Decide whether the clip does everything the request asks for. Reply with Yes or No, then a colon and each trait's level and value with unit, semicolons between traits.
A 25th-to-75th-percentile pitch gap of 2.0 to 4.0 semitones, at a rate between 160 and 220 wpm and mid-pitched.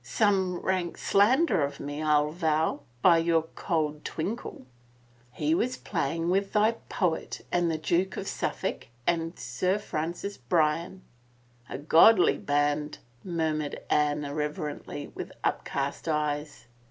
No: average, 3.5 semitones; average, 145 wpm; medium, 155 Hz